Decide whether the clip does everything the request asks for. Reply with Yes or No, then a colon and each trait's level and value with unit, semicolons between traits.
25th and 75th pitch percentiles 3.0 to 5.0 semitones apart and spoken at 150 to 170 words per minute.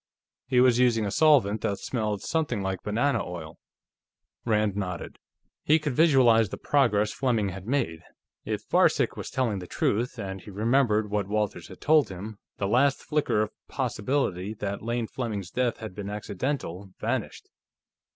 Yes: average, 4.2 semitones; average, 160 wpm